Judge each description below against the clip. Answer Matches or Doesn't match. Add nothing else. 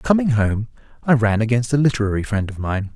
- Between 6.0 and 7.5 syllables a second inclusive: Doesn't match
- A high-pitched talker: Doesn't match